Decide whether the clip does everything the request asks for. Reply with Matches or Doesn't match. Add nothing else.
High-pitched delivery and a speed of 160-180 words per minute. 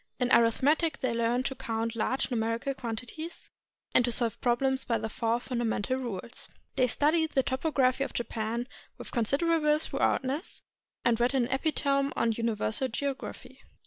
Doesn't match